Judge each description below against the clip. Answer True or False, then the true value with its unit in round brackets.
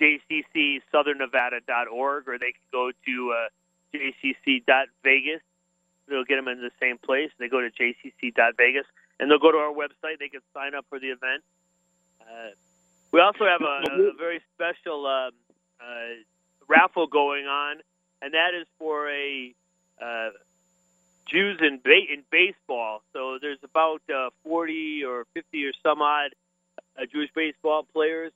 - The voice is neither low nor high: True (145 Hz)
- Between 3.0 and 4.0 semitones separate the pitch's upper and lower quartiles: False (4.5 semitones)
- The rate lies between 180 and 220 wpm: False (150 wpm)